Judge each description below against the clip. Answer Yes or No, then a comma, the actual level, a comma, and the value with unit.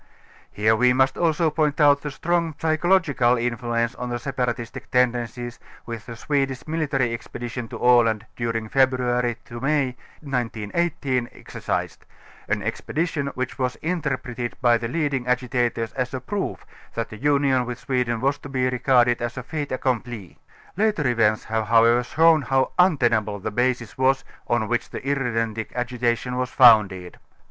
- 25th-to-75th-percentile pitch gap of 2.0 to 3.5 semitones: Yes, average, 2.8 semitones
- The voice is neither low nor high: No, low, 125 Hz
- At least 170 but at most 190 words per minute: No, average, 155 wpm